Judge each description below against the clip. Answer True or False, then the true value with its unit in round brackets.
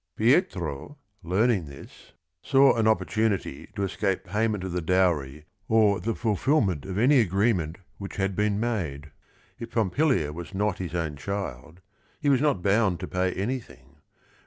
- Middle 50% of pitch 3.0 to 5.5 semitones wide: True (4.4 semitones)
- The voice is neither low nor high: False (100 Hz)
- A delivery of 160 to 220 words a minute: False (150 wpm)